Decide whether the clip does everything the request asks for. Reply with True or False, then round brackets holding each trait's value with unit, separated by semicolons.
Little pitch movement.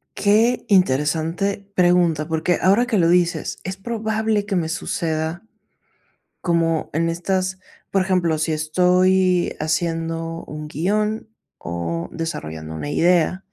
False (3.1 semitones)